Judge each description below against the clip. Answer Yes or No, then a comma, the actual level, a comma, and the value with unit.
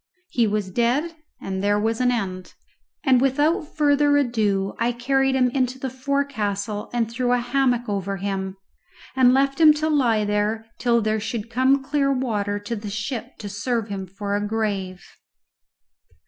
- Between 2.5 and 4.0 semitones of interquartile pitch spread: No, average, 4.4 semitones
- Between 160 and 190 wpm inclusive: Yes, average, 165 wpm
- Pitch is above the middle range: Yes, high, 235 Hz